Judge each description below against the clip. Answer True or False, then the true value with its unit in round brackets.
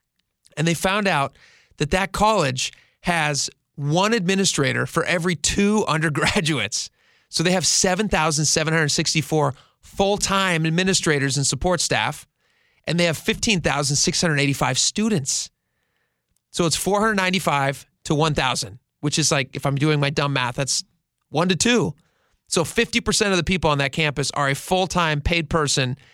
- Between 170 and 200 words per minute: False (140 wpm)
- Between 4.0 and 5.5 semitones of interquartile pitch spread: True (4.6 semitones)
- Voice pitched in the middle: True (160 Hz)